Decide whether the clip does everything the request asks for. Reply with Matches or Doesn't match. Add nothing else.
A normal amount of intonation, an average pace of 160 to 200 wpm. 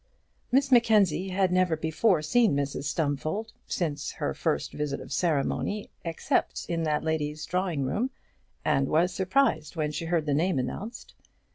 Doesn't match